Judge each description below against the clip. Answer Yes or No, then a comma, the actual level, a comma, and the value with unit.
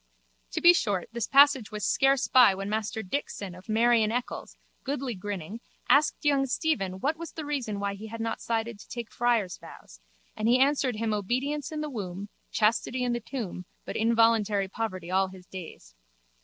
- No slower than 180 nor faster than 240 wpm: Yes, average, 185 wpm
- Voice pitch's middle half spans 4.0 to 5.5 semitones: Yes, average, 4.4 semitones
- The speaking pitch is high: Yes, high, 225 Hz